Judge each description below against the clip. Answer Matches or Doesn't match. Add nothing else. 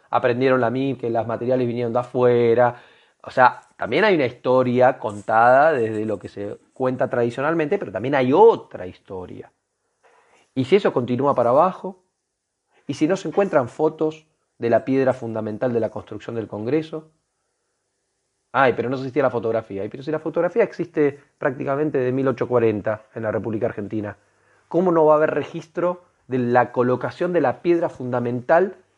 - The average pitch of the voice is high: Doesn't match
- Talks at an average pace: Matches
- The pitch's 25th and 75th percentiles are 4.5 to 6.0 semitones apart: Matches